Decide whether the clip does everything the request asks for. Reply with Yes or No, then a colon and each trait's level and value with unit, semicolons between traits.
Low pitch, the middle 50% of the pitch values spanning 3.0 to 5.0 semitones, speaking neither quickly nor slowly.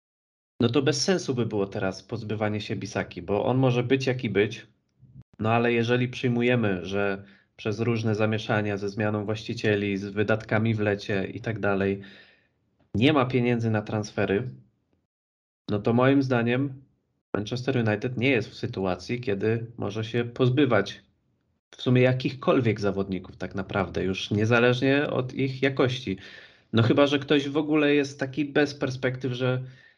Yes: low, 115 Hz; average, 4.2 semitones; average, 150 wpm